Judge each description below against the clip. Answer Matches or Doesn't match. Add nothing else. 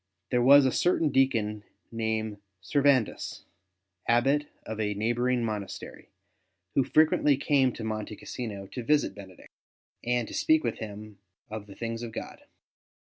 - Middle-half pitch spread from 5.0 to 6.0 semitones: Doesn't match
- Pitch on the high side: Doesn't match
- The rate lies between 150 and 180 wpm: Doesn't match